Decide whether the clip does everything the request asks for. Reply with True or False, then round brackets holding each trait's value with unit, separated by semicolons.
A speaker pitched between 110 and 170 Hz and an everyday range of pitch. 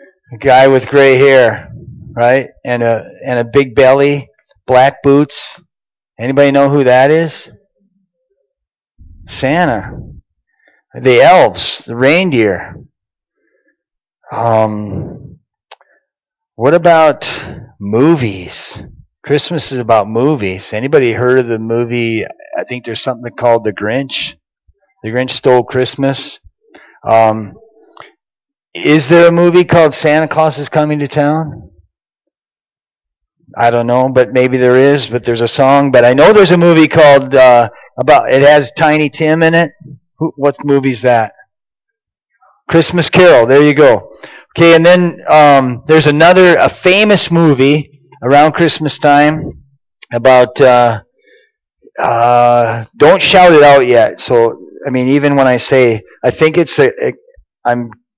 True (140 Hz; 4.6 semitones)